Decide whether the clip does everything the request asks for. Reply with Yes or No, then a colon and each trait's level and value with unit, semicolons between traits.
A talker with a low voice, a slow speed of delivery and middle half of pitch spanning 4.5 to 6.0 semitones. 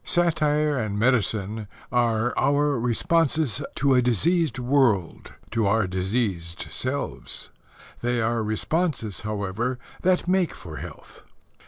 Yes: low, 120 Hz; slow, 115 wpm; average, 5.2 semitones